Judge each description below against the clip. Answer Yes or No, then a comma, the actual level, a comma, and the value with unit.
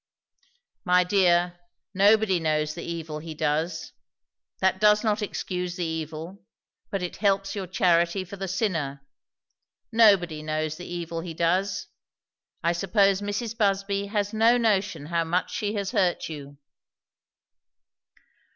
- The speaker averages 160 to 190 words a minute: No, slow, 135 wpm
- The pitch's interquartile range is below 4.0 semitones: Yes, average, 3.4 semitones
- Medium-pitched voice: Yes, medium, 180 Hz